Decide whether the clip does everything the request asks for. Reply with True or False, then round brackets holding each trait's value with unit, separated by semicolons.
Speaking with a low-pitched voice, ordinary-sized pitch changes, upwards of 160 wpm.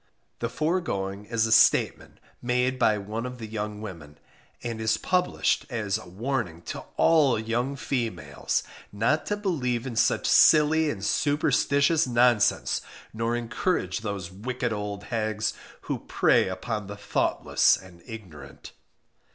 False (115 Hz; 3.8 semitones; 135 wpm)